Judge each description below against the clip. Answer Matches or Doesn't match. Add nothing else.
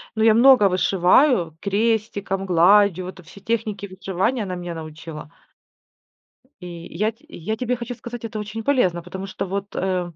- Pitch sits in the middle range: Doesn't match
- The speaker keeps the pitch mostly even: Doesn't match